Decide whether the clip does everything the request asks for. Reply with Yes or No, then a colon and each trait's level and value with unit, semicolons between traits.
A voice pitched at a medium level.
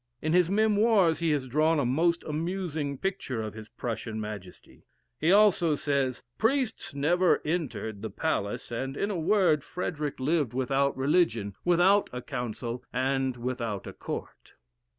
Yes: medium, 145 Hz